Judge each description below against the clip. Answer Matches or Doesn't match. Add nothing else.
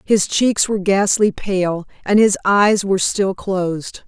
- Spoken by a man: Doesn't match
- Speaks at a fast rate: Doesn't match